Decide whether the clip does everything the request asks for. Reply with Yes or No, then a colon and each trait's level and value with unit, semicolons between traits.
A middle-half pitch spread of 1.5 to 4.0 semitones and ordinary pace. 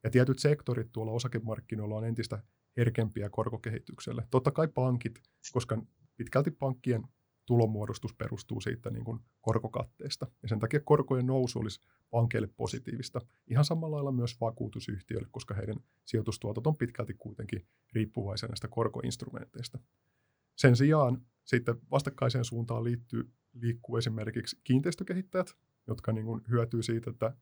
Yes: narrow, 2.4 semitones; average, 125 wpm